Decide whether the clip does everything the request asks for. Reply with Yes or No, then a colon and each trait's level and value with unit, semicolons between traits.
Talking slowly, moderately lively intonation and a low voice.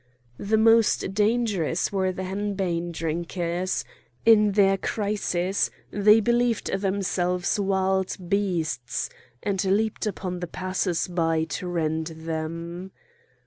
No: slow, 105 wpm; average, 3.1 semitones; high, 190 Hz